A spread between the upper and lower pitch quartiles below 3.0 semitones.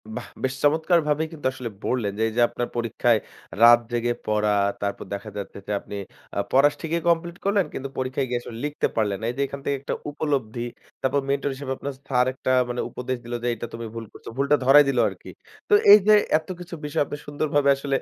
No: average, 3.7 semitones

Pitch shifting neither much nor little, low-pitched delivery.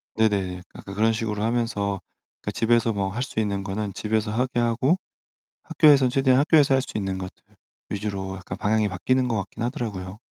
Yes: average, 3.6 semitones; low, 110 Hz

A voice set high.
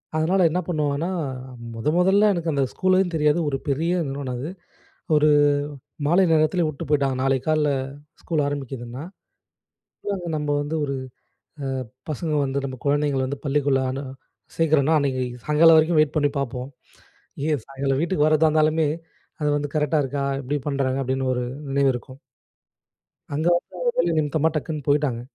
No: medium, 145 Hz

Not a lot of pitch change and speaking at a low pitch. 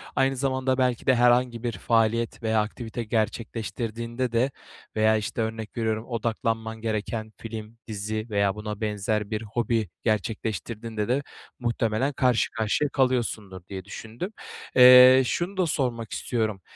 Yes: narrow, 2.3 semitones; low, 115 Hz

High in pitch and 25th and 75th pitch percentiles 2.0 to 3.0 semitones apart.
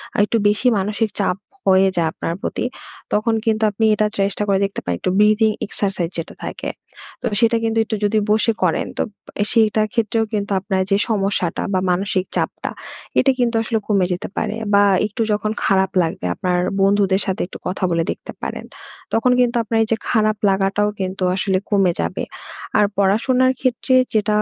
Yes: high, 205 Hz; narrow, 2.5 semitones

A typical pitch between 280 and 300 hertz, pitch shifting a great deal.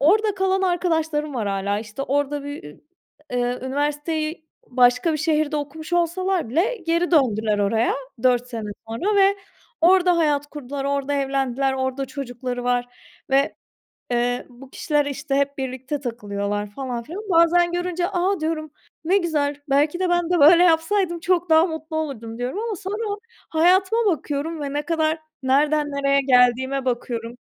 No: very high, 290 Hz; average, 4.9 semitones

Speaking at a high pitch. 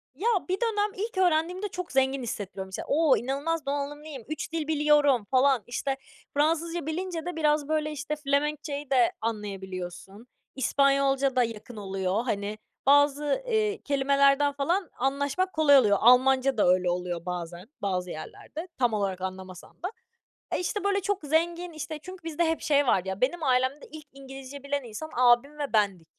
Yes: very high, 280 Hz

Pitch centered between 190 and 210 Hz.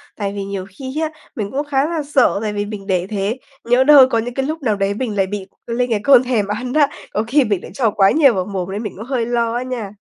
No: high, 230 Hz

